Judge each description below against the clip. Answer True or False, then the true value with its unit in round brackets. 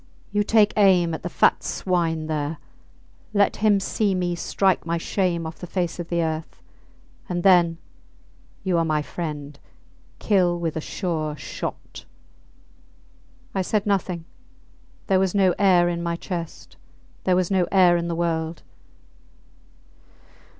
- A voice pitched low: False (175 Hz)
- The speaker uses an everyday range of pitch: False (2.3 semitones)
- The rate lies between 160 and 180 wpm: False (145 wpm)